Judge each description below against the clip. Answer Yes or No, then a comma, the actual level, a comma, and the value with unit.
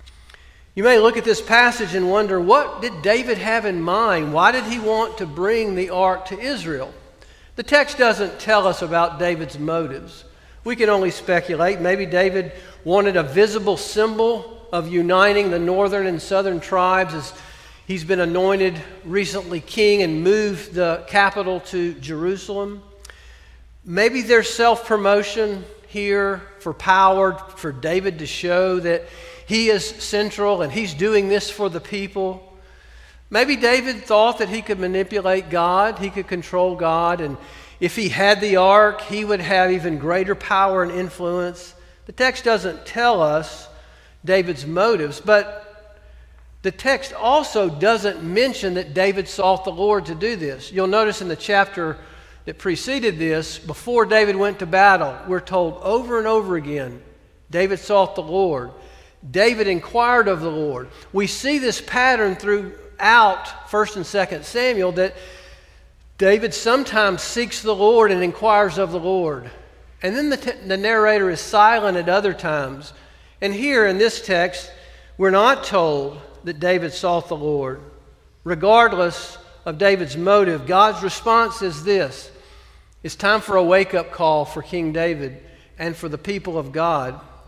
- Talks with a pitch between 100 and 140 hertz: No, high, 190 Hz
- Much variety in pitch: No, average, 3.5 semitones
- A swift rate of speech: No, average, 155 wpm